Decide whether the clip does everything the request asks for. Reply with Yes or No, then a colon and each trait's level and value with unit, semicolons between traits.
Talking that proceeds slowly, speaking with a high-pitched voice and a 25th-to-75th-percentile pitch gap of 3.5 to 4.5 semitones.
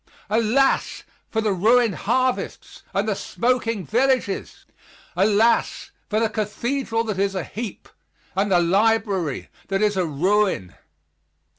No: slow, 125 wpm; high, 215 Hz; average, 3.0 semitones